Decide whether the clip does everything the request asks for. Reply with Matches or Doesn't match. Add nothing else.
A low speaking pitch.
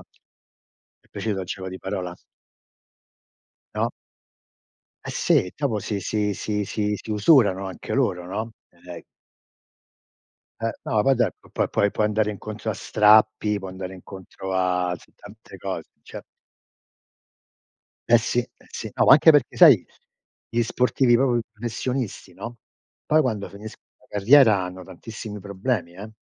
Matches